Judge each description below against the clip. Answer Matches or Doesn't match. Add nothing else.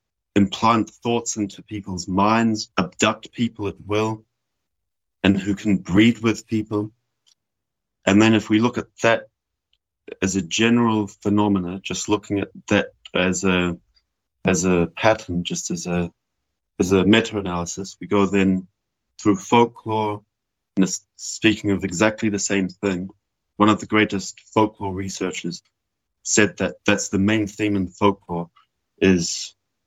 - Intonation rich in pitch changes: Doesn't match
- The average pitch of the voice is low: Matches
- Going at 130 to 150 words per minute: Matches